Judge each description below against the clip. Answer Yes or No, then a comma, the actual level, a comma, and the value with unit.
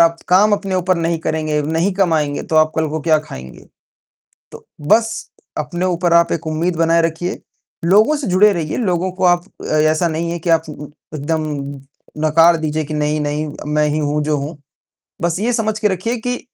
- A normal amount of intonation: Yes, average, 3.0 semitones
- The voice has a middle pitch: Yes, medium, 165 Hz